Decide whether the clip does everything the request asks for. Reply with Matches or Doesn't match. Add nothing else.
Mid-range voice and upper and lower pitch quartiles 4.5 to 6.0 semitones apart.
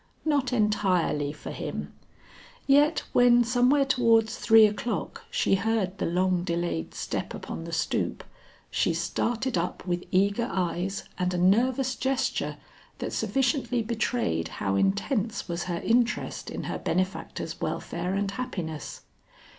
Doesn't match